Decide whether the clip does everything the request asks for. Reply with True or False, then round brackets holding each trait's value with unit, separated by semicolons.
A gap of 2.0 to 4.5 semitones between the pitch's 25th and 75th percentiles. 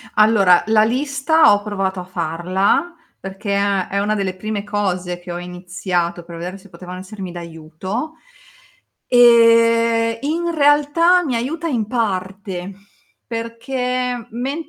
False (5.0 semitones)